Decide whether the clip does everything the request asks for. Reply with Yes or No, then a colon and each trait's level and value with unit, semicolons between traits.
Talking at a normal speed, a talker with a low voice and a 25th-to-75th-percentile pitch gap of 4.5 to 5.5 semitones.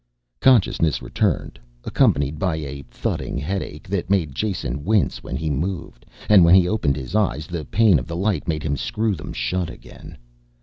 Yes: average, 175 wpm; very low, 85 Hz; average, 4.9 semitones